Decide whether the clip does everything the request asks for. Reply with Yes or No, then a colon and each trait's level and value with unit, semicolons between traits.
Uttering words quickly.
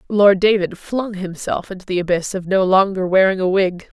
No: average, 195 wpm